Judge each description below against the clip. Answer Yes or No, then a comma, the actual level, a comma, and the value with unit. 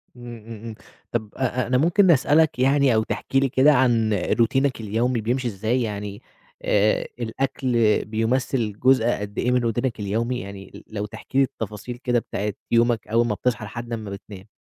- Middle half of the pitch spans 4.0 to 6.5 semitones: No, average, 3.0 semitones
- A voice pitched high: No, low, 115 Hz